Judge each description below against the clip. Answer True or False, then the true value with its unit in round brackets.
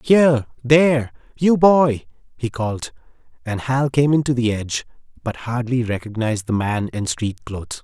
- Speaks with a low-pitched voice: True (125 Hz)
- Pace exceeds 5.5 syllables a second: False (5.0 syllables/s)